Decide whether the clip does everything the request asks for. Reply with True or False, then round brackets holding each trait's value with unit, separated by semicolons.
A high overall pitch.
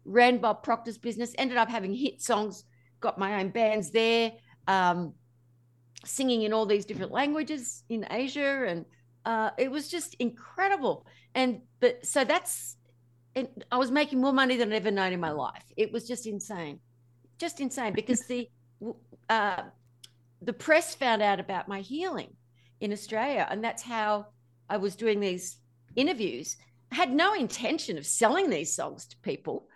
True (220 Hz)